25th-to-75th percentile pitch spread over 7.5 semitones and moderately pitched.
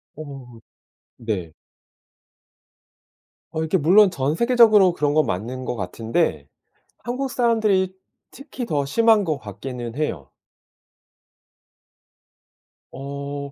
Yes: wide, 8.5 semitones; medium, 145 Hz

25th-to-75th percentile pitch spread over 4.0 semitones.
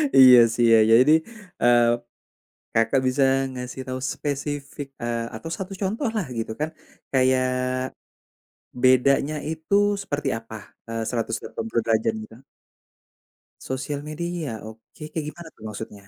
Yes: average, 4.5 semitones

